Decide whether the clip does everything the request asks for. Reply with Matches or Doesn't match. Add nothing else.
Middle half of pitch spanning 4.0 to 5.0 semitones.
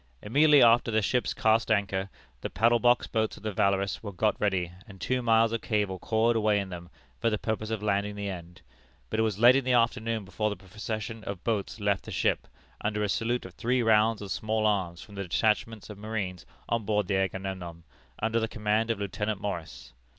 Doesn't match